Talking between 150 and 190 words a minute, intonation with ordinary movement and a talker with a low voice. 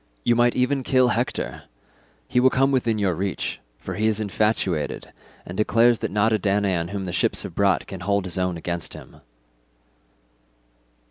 Yes: average, 175 wpm; average, 4.3 semitones; low, 105 Hz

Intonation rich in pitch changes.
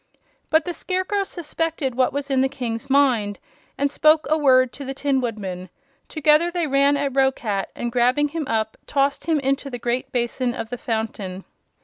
No: average, 3.6 semitones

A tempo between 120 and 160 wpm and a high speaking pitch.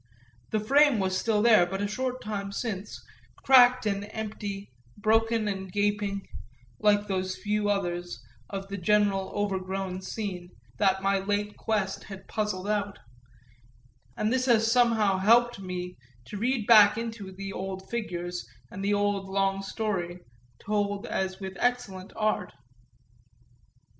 Yes: average, 140 wpm; high, 205 Hz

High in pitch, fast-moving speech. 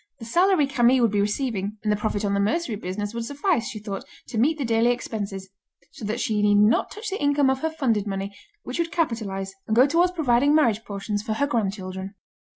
Yes: high, 225 Hz; fast, 220 wpm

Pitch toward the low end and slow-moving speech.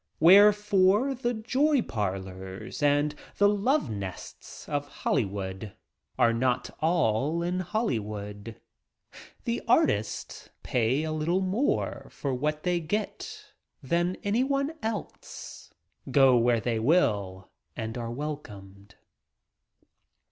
No: medium, 145 Hz; slow, 105 wpm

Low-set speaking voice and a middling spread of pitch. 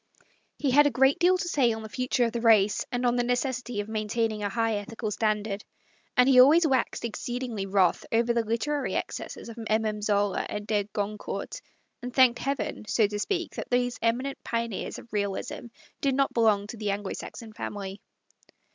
No: high, 230 Hz; average, 3.0 semitones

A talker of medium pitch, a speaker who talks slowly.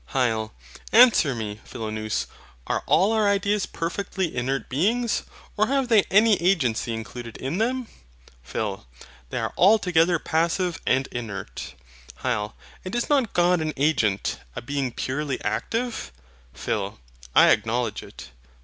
Yes: medium, 155 Hz; slow, 130 wpm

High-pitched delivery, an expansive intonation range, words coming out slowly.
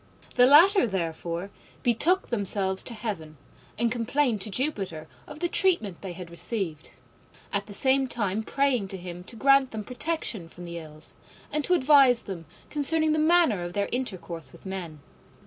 No: high, 215 Hz; wide, 7.5 semitones; average, 165 wpm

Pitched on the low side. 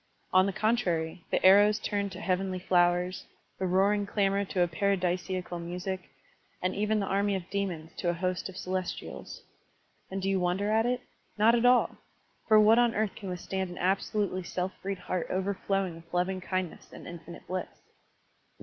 No: high, 190 Hz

